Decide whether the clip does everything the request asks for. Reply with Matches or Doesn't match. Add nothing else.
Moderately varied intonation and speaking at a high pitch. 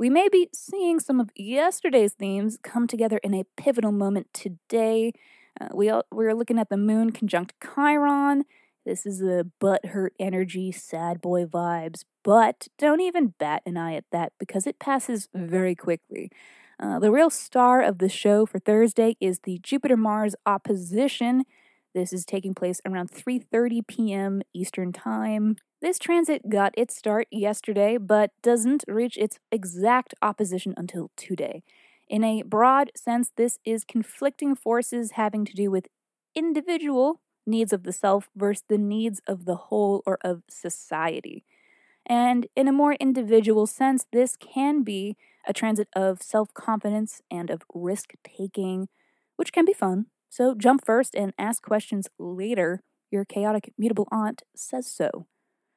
Matches